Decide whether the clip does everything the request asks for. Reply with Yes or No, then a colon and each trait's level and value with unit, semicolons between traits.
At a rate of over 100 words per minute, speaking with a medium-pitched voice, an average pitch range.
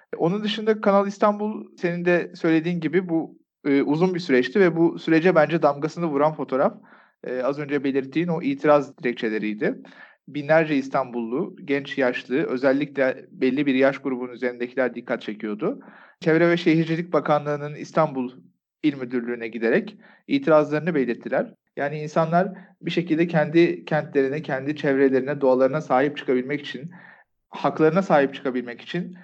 Yes: average, 135 wpm; medium, 150 Hz; average, 4.2 semitones